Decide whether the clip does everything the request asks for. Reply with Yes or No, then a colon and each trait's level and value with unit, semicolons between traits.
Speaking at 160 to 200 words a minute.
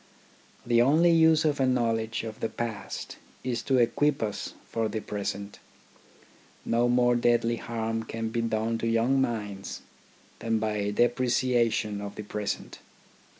No: average, 145 wpm